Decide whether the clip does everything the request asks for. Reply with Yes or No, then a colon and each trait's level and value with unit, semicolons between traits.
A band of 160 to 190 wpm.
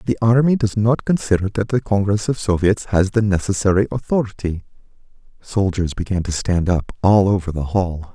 Yes: average, 170 wpm